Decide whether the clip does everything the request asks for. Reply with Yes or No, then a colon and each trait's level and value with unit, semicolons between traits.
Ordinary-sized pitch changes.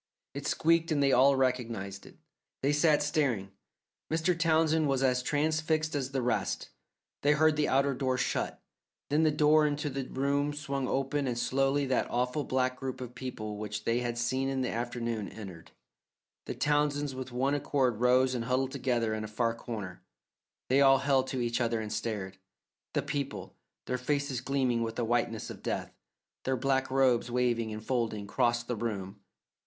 Yes: average, 3.3 semitones